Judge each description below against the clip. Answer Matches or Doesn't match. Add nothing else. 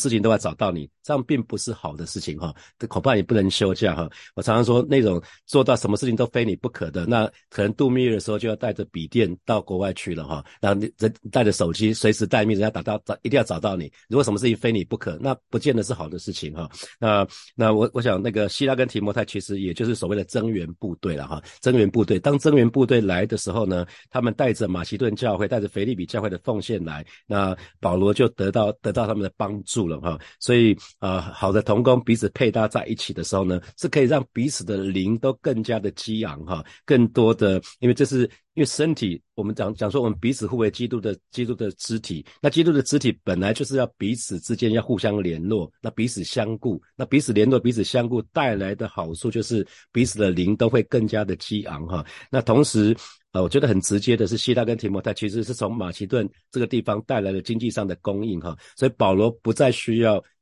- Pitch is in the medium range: Doesn't match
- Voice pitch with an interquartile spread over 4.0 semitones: Doesn't match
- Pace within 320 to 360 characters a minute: Matches